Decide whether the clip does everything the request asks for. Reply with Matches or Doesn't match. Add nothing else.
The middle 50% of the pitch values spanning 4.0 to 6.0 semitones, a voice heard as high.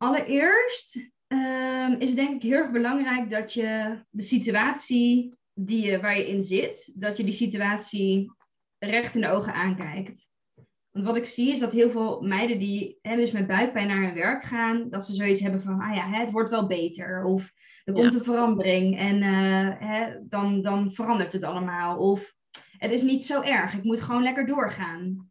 Doesn't match